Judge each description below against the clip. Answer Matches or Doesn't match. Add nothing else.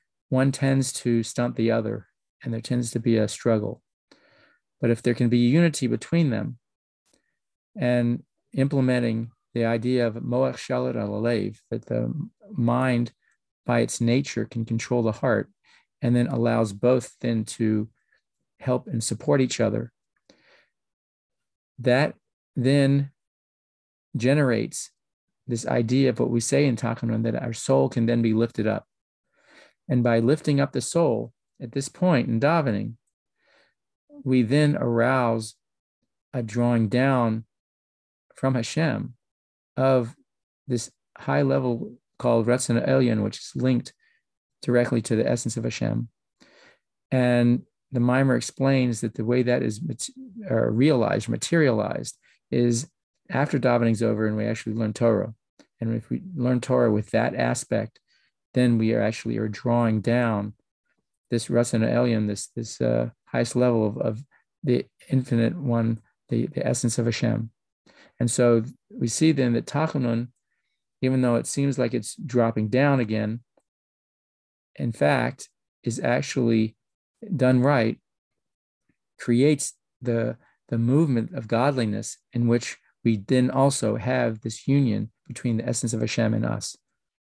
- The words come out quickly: Doesn't match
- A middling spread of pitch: Doesn't match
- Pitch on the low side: Matches